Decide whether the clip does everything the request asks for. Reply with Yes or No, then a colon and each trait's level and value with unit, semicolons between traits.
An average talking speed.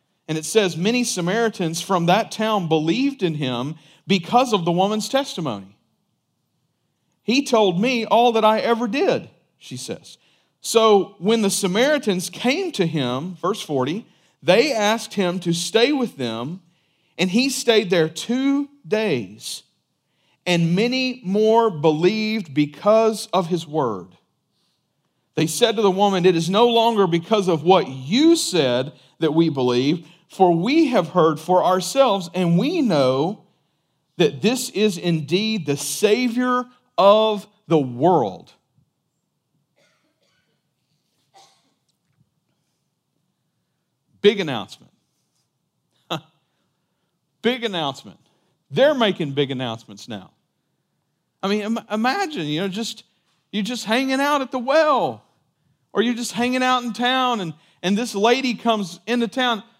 No: slow, 130 wpm